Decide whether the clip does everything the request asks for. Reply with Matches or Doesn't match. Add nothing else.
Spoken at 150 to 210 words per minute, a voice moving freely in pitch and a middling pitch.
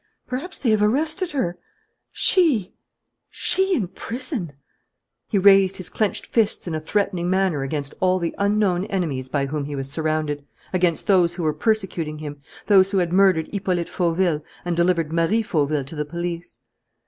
Doesn't match